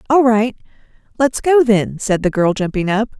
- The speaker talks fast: No, average, 190 wpm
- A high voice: Yes, high, 225 Hz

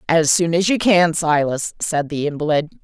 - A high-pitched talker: No, medium, 165 Hz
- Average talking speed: Yes, average, 190 wpm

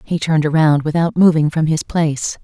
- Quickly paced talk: No, average, 195 wpm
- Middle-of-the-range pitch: Yes, medium, 155 Hz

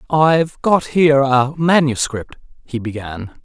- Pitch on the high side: No, medium, 140 Hz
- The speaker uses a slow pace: Yes, slow, 120 wpm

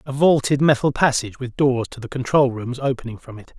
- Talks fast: Yes, fast, 215 wpm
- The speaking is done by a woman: No, male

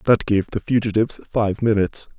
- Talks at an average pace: Yes, average, 165 wpm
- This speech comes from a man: Yes, male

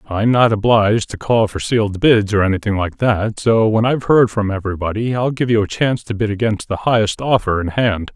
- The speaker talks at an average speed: No, fast, 230 wpm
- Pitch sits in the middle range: No, low, 110 Hz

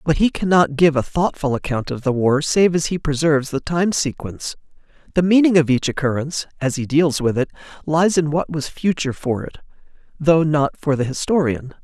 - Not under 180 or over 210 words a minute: Yes, average, 200 wpm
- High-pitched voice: No, medium, 150 Hz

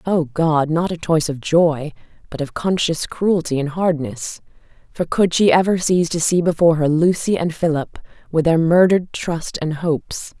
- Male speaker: No, female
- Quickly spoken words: No, average, 180 wpm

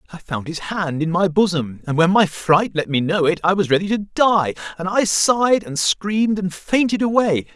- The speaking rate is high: Yes, fast, 220 wpm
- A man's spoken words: Yes, male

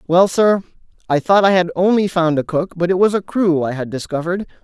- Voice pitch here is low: No, medium, 175 Hz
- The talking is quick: Yes, fast, 235 wpm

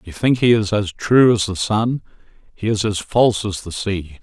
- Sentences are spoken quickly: Yes, fast, 215 wpm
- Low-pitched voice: Yes, low, 105 Hz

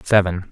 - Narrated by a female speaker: No, male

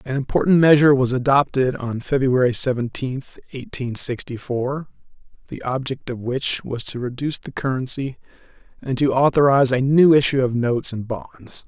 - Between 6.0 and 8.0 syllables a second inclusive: No, 5.1 syllables/s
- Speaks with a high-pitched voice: No, low, 130 Hz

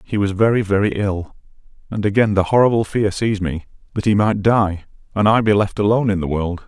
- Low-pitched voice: Yes, low, 100 Hz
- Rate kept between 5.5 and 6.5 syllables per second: Yes, 5.9 syllables/s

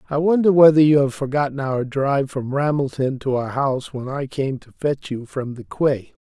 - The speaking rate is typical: No, fast, 210 wpm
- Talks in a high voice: No, medium, 140 Hz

